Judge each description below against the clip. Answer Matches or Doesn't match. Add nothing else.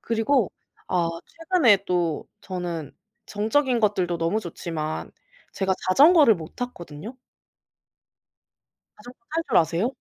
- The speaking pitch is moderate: Doesn't match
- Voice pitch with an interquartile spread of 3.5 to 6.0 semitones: Doesn't match